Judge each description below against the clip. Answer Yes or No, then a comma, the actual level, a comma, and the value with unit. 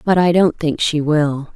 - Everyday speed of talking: No, fast, 230 wpm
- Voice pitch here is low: No, medium, 160 Hz